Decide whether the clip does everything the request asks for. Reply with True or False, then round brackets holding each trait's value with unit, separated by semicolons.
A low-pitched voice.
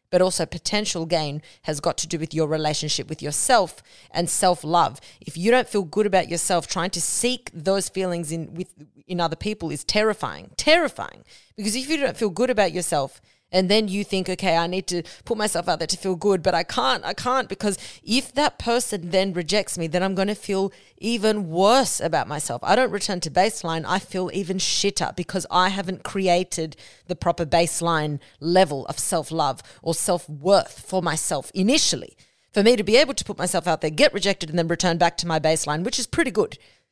False (180 Hz)